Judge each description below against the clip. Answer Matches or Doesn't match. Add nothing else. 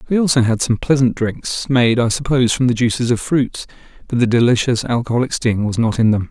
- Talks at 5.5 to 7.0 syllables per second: Matches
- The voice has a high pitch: Doesn't match